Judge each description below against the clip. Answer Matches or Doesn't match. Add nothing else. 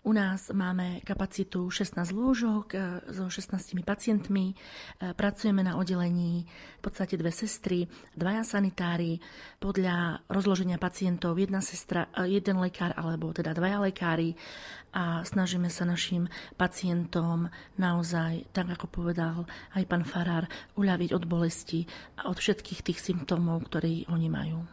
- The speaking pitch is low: Doesn't match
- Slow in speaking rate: Doesn't match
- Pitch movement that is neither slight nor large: Doesn't match